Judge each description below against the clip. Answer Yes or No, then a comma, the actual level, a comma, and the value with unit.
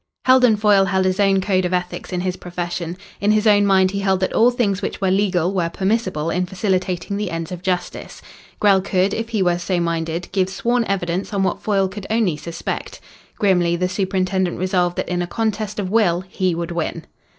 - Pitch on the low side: No, high, 190 Hz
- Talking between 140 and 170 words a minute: No, fast, 205 wpm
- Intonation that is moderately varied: No, narrow, 2.2 semitones